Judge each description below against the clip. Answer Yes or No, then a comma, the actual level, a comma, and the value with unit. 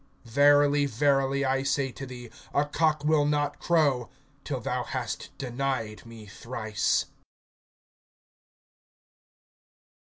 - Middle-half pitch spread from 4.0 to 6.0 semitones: No, average, 3.0 semitones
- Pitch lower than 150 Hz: Yes, low, 135 Hz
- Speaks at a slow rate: Yes, slow, 100 wpm